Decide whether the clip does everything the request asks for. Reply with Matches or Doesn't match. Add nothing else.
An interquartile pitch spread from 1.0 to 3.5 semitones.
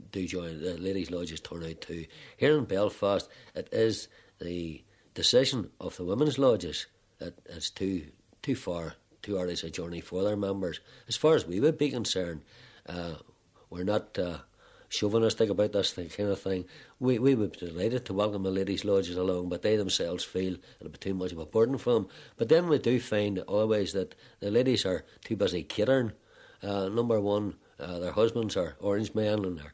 Doesn't match